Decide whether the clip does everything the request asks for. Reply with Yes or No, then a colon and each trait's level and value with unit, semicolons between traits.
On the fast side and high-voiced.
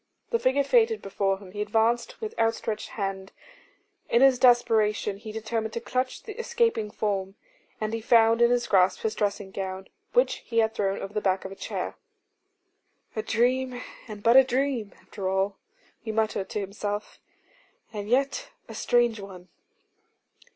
No: average, 165 wpm; high, 220 Hz